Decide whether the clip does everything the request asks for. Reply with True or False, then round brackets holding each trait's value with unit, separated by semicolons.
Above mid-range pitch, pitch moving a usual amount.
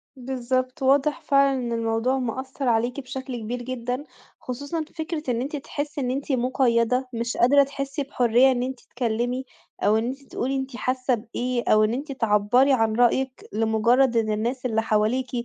False (255 Hz; 2.3 semitones)